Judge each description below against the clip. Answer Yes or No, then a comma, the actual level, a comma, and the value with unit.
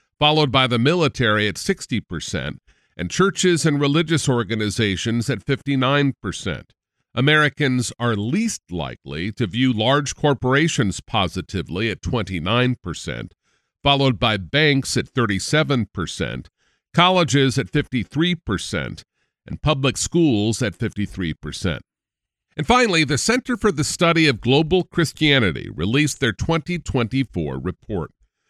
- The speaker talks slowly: Yes, slow, 105 wpm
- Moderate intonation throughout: No, wide, 6.3 semitones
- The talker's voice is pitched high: No, low, 130 Hz